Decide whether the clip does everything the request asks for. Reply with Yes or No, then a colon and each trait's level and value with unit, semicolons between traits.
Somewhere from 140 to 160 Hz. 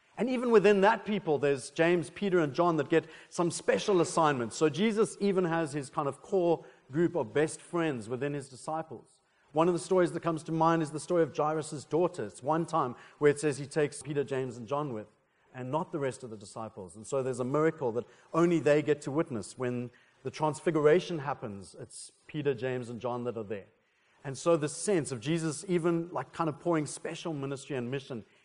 Yes: medium, 150 Hz